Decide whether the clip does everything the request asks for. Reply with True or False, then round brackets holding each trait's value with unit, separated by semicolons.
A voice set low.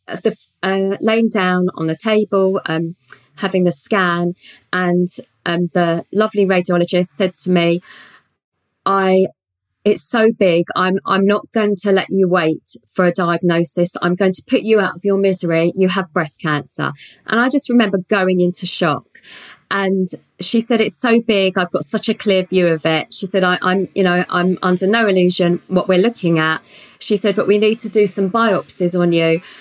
False (185 Hz)